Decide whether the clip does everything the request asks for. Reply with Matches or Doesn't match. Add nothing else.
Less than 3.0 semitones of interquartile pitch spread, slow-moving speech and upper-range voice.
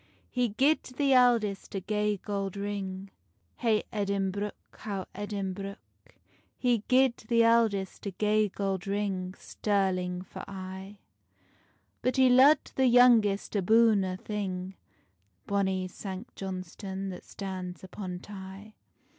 Matches